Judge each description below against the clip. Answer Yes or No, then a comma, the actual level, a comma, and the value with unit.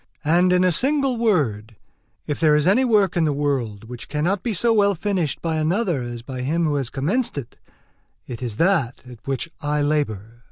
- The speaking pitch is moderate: Yes, medium, 155 Hz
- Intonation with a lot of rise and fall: Yes, wide, 6.8 semitones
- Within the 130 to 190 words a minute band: No, average, 200 wpm